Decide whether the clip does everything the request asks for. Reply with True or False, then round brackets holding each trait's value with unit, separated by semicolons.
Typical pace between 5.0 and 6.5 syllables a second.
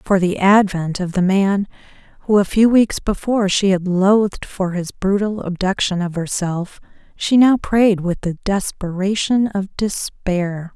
False (4.1 syllables/s)